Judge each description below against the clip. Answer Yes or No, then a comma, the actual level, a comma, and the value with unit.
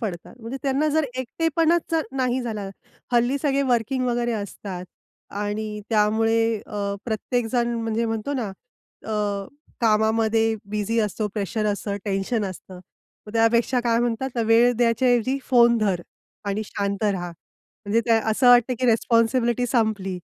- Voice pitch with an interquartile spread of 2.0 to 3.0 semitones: Yes, average, 2.7 semitones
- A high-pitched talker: Yes, high, 225 Hz